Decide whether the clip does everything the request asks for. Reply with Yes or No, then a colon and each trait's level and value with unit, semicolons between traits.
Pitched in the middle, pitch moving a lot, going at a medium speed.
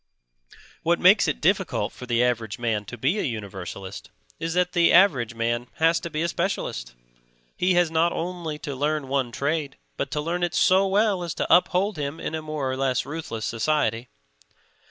Yes: medium, 150 Hz; wide, 6.2 semitones; average, 190 wpm